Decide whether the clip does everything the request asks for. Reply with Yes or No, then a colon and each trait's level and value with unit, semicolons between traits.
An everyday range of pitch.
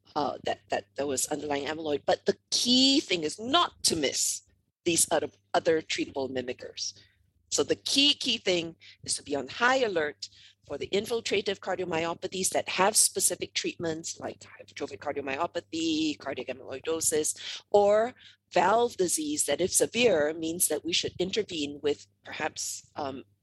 No: wide, 7.1 semitones